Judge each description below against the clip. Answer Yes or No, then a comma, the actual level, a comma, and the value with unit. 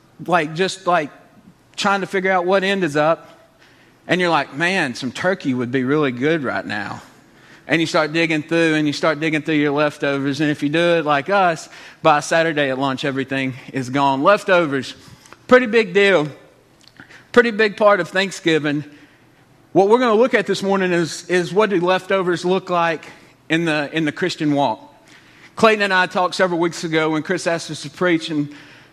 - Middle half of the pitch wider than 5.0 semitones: No, average, 4.0 semitones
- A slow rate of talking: No, average, 195 wpm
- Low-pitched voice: No, medium, 165 Hz